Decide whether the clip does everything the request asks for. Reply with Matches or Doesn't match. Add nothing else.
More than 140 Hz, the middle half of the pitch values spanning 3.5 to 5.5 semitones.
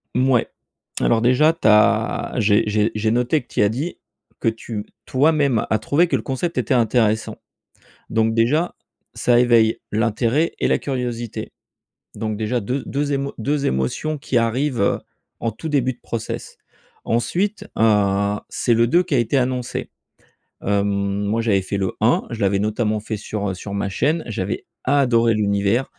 Doesn't match